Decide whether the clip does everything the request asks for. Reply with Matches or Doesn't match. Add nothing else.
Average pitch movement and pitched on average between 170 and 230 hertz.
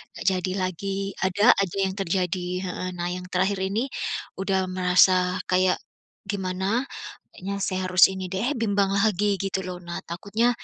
Doesn't match